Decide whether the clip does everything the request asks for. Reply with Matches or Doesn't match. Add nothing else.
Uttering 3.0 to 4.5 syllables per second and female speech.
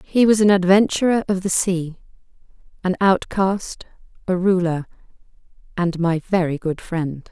Matches